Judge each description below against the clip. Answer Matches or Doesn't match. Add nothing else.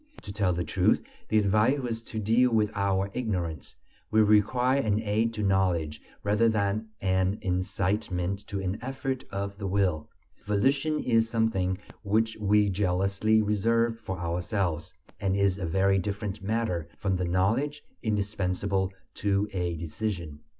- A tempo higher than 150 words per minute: Doesn't match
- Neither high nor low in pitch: Doesn't match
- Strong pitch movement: Doesn't match